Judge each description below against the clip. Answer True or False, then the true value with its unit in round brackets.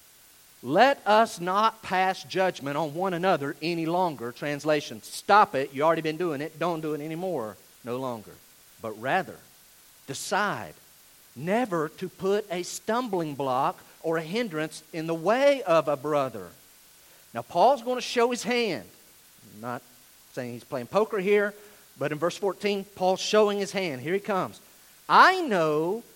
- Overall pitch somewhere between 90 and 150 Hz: False (180 Hz)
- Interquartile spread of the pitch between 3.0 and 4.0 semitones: False (4.9 semitones)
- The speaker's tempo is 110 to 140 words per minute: False (160 wpm)